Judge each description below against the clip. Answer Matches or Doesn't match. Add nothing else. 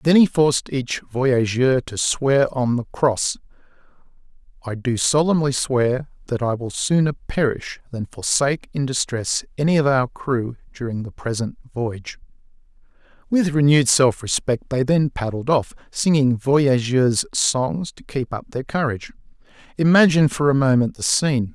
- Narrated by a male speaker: Matches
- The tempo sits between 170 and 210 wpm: Doesn't match